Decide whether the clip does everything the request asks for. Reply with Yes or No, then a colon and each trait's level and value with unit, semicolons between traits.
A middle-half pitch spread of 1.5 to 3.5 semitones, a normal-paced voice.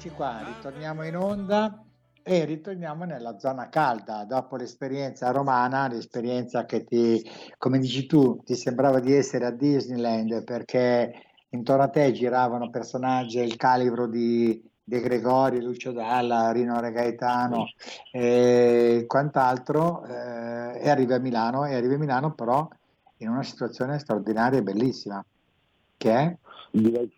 Yes: narrow, 2.4 semitones; average, 130 wpm